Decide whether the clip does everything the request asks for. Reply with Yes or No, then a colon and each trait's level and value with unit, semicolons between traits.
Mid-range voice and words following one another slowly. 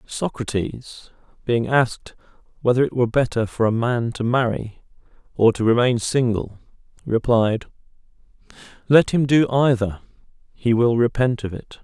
No: low, 120 Hz; slow, 125 wpm